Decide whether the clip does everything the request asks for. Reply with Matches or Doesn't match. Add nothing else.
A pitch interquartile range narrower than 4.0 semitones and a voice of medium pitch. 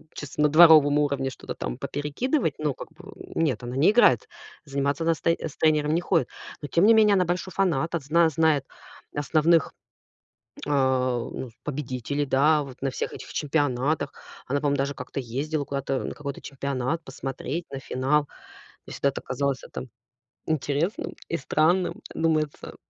Matches